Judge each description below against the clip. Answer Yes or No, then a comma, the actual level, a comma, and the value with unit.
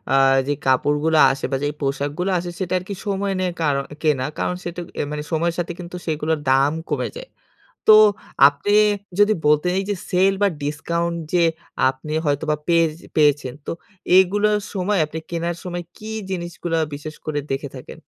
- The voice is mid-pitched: Yes, medium, 165 Hz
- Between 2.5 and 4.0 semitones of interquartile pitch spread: Yes, average, 3.5 semitones